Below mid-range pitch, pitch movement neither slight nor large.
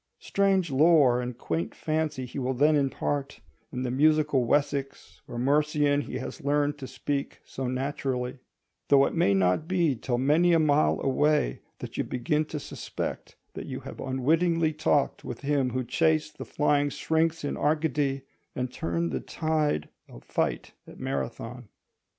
No: medium, 145 Hz; average, 3.3 semitones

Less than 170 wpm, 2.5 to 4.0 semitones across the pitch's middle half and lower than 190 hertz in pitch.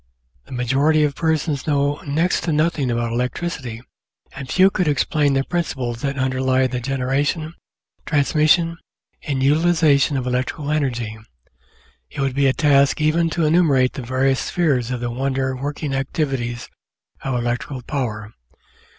Yes: average, 140 wpm; average, 3.1 semitones; medium, 140 Hz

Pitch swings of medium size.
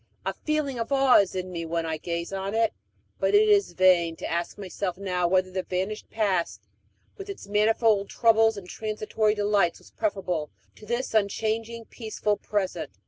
Yes: average, 3.6 semitones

